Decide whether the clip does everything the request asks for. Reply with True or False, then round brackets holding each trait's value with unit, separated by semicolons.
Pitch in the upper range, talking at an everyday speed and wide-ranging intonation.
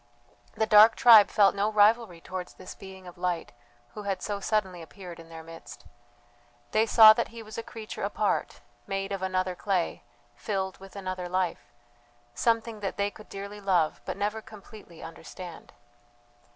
False (195 Hz; 165 wpm; 2.7 semitones)